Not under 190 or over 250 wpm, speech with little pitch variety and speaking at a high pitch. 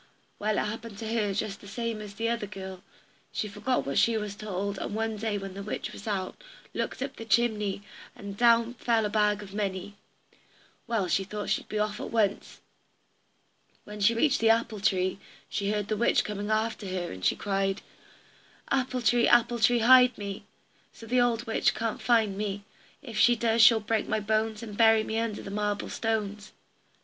Yes: average, 200 wpm; narrow, 2.1 semitones; high, 215 Hz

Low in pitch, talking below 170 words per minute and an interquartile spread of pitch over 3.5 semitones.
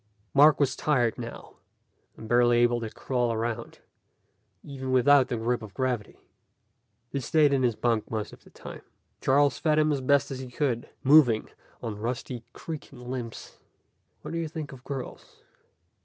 No: low, 130 Hz; average, 160 wpm; average, 3.1 semitones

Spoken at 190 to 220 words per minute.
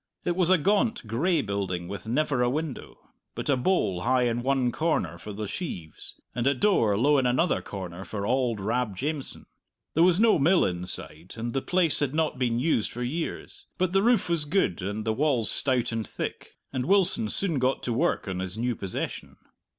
Yes: average, 200 wpm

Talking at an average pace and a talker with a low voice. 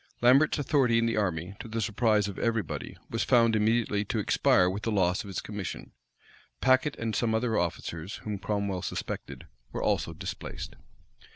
Yes: average, 175 wpm; low, 110 Hz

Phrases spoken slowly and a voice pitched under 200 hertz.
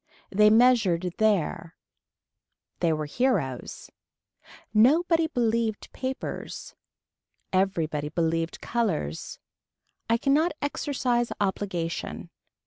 No: slow, 75 wpm; high, 210 Hz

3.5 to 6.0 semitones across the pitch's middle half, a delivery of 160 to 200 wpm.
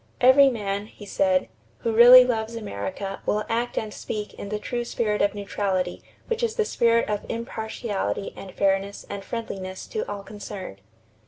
No: average, 2.9 semitones; average, 165 wpm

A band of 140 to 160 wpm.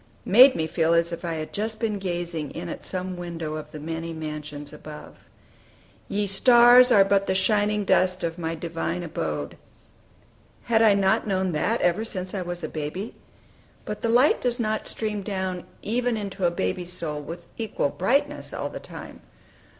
No: average, 180 wpm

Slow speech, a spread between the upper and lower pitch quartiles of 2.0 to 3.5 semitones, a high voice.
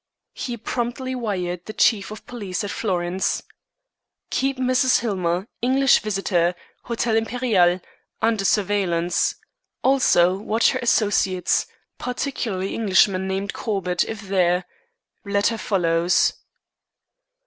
No: slow, 105 wpm; average, 4.3 semitones; high, 200 Hz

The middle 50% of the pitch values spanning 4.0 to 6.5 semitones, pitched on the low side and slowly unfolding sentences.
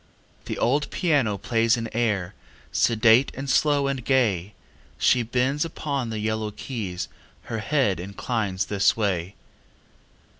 Yes: average, 4.5 semitones; low, 115 Hz; slow, 125 wpm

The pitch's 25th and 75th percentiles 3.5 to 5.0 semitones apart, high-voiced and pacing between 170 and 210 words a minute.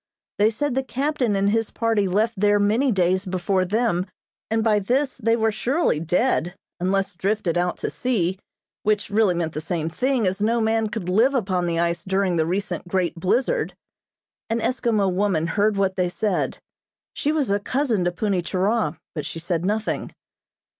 Yes: average, 3.9 semitones; high, 205 Hz; average, 180 wpm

